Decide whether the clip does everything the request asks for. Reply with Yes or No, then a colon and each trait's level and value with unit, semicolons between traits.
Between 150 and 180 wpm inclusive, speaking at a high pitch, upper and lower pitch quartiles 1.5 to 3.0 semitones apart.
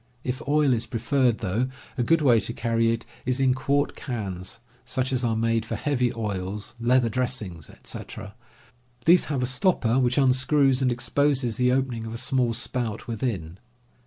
No: average, 170 wpm; low, 125 Hz; narrow, 2.6 semitones